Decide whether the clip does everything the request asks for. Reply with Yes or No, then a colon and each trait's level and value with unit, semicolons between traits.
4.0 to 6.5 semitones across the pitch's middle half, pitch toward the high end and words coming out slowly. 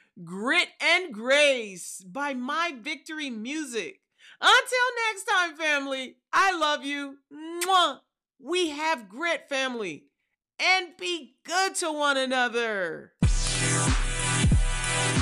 Yes: average, 5.0 semitones; very high, 310 Hz; slow, 100 wpm